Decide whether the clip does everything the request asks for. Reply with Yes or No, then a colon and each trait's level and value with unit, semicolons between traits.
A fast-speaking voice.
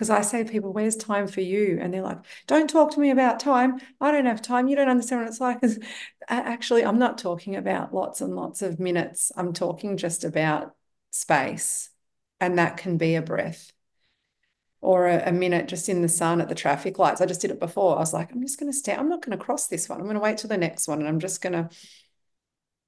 Yes: fast, 240 wpm